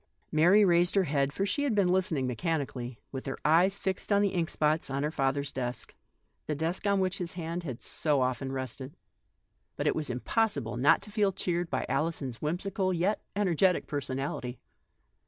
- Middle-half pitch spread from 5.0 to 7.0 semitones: Yes, wide, 5.6 semitones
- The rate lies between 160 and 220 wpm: Yes, average, 185 wpm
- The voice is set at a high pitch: No, medium, 160 Hz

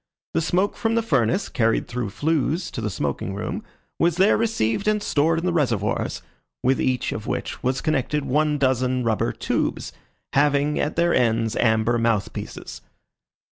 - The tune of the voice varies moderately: No, wide, 6.2 semitones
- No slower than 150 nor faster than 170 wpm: Yes, average, 165 wpm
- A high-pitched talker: No, low, 135 Hz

